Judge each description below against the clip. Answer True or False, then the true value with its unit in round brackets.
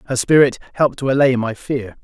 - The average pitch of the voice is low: True (130 Hz)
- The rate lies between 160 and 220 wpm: True (205 wpm)